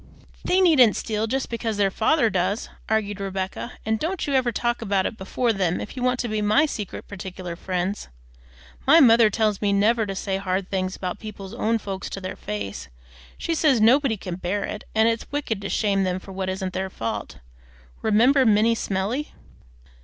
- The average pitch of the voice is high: Yes, high, 210 Hz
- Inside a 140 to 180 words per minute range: No, average, 190 wpm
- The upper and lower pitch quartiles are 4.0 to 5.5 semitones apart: No, average, 3.6 semitones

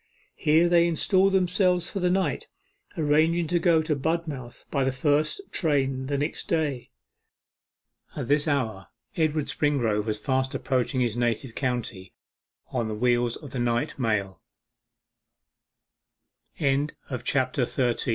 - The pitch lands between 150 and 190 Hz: No, medium, 140 Hz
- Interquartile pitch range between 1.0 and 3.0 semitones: No, average, 5.1 semitones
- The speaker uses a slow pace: Yes, slow, 120 wpm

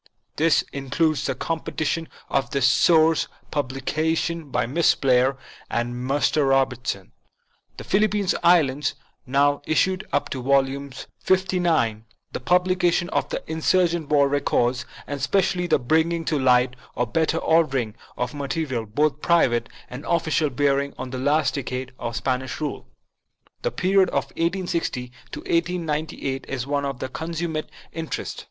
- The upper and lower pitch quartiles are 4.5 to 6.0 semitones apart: No, average, 4.1 semitones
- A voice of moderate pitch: Yes, medium, 145 Hz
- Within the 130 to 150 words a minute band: Yes, average, 140 wpm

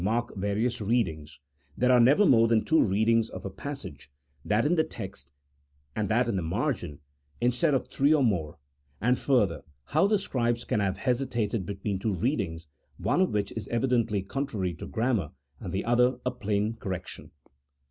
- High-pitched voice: No, low, 115 Hz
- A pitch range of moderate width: Yes, average, 4.4 semitones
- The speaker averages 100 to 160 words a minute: No, average, 175 wpm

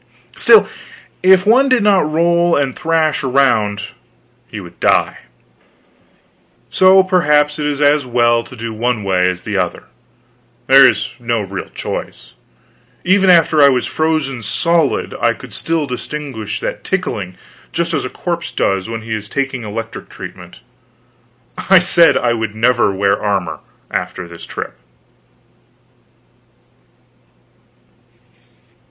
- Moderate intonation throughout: No, wide, 7.1 semitones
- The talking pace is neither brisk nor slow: No, slow, 130 wpm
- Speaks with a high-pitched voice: No, low, 135 Hz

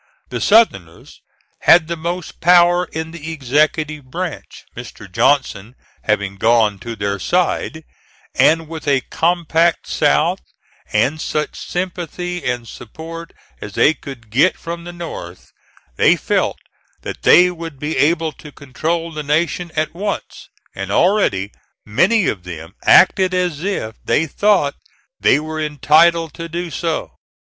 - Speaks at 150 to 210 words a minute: No, slow, 135 wpm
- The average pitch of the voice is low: No, medium, 160 Hz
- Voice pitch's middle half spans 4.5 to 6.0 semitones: Yes, average, 4.8 semitones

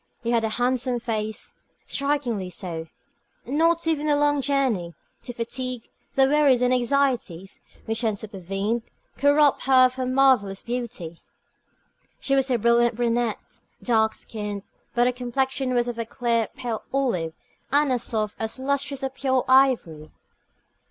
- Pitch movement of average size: Yes, average, 3.4 semitones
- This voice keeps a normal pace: Yes, average, 150 wpm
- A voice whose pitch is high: Yes, high, 245 Hz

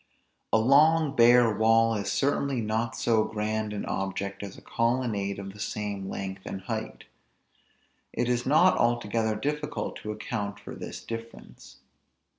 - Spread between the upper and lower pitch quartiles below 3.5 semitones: Yes, average, 3.0 semitones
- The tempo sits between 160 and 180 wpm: No, average, 145 wpm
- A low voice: Yes, low, 110 Hz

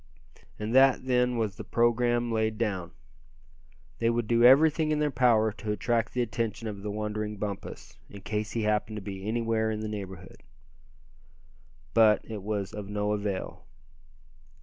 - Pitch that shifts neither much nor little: No, narrow, 2.2 semitones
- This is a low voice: Yes, low, 110 Hz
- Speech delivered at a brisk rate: No, average, 165 wpm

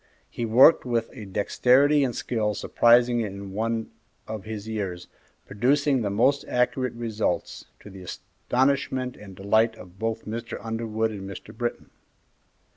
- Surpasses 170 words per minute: No, average, 140 wpm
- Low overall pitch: Yes, low, 115 Hz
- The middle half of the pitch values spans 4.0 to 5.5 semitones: No, average, 3.0 semitones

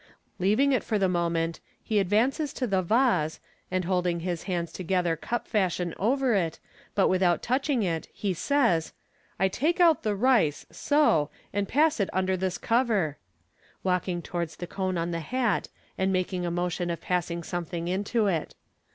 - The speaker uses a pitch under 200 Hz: Yes, medium, 185 Hz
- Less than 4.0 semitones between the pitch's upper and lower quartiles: No, average, 4.7 semitones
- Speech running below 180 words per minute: Yes, average, 170 wpm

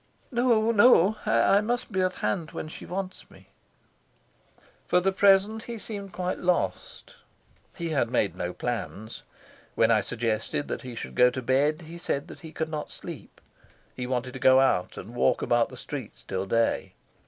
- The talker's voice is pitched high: No, medium, 155 Hz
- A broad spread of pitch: Yes, wide, 8.2 semitones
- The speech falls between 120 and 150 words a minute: No, average, 175 wpm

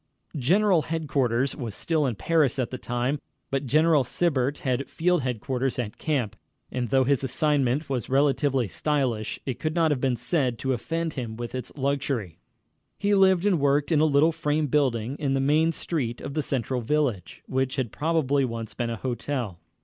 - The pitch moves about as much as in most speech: Yes, average, 3.7 semitones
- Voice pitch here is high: No, low, 135 Hz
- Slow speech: No, average, 180 wpm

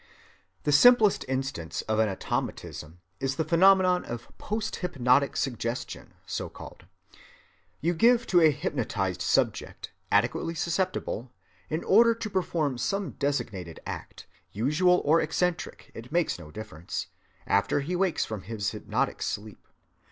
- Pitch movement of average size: No, wide, 8.3 semitones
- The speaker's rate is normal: No, slow, 120 wpm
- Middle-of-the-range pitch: Yes, medium, 145 Hz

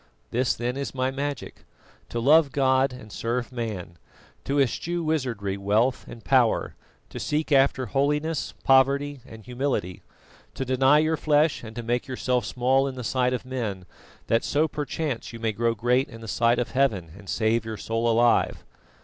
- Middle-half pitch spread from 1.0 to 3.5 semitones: Yes, average, 3.2 semitones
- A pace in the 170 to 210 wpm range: Yes, average, 175 wpm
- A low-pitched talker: Yes, low, 125 Hz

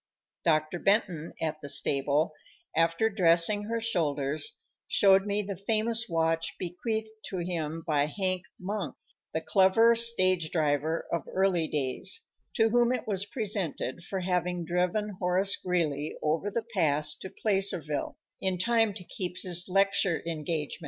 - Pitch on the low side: No, medium, 180 Hz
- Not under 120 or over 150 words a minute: Yes, average, 140 wpm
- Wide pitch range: No, average, 4.0 semitones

